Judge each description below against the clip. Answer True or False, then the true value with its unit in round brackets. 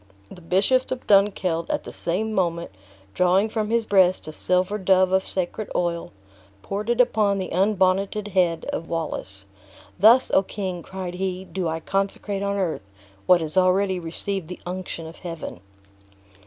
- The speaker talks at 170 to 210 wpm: False (160 wpm)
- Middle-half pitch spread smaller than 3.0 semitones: True (2.4 semitones)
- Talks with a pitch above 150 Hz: True (185 Hz)